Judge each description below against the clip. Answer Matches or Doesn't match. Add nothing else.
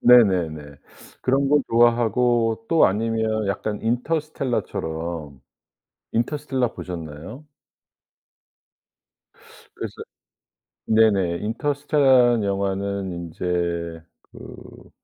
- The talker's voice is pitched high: Doesn't match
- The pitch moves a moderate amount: Doesn't match